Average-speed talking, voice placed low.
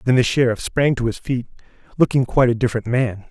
No: fast, 220 wpm; low, 120 Hz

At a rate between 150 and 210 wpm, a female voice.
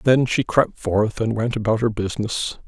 No: average, 200 wpm; male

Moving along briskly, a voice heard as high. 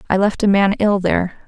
Yes: fast, 245 wpm; high, 195 Hz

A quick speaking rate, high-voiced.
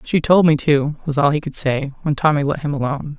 No: fast, 265 wpm; medium, 145 Hz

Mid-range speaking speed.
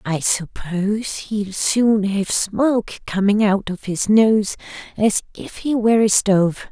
Yes: average, 150 wpm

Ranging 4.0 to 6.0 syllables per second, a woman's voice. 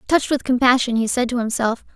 No: 6.4 syllables/s; female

